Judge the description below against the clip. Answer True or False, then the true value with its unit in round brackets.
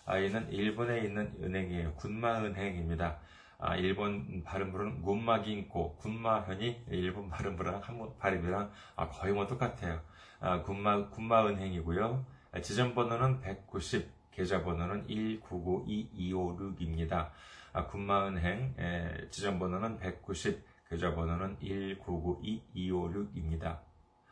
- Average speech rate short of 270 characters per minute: True (245 characters per minute)